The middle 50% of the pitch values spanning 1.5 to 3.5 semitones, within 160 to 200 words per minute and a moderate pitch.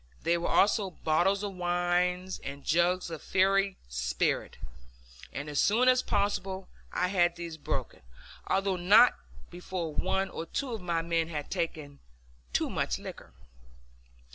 No: average, 2.8 semitones; average, 140 wpm; medium, 180 Hz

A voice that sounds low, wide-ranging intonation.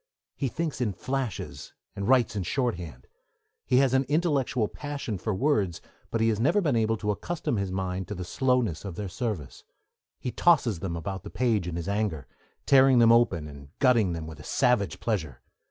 Yes: low, 110 Hz; wide, 5.8 semitones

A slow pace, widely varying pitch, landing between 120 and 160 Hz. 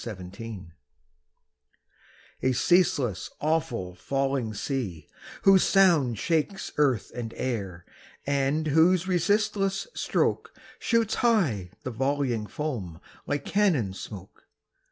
Yes: slow, 95 wpm; wide, 8.1 semitones; low, 135 Hz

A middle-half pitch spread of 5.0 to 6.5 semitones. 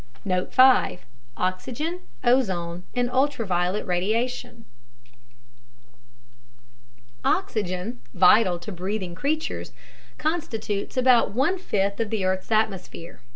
Yes: wide, 5.5 semitones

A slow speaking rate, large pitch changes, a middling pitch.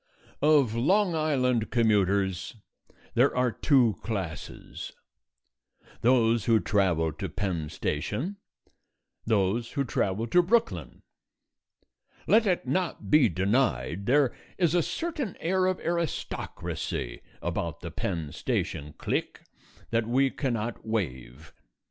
No: slow, 110 wpm; wide, 7.7 semitones; low, 115 Hz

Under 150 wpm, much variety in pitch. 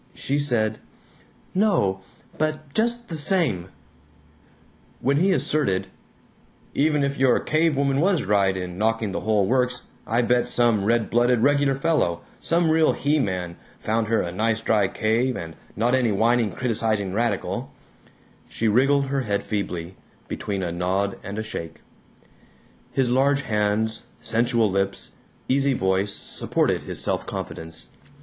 Yes: average, 140 wpm; wide, 5.7 semitones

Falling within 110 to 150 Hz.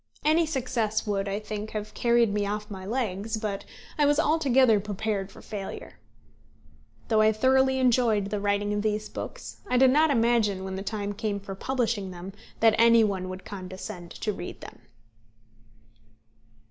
No: high, 215 Hz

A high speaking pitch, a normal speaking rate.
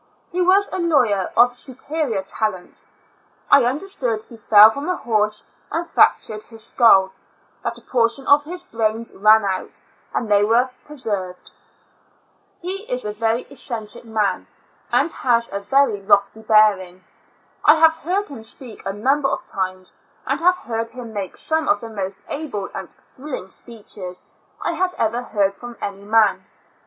Yes: high, 230 Hz; average, 160 wpm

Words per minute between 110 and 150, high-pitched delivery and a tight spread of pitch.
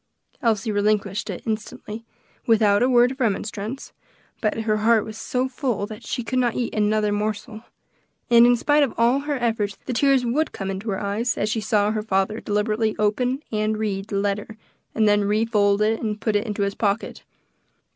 No: average, 185 wpm; high, 215 Hz; narrow, 2.3 semitones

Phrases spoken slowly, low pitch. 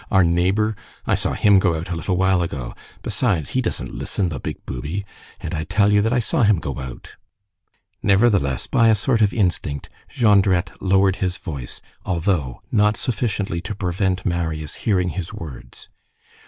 No: average, 170 wpm; very low, 95 Hz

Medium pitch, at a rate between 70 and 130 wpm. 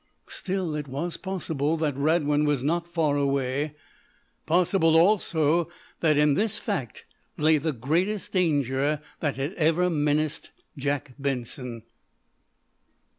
Yes: medium, 150 Hz; slow, 120 wpm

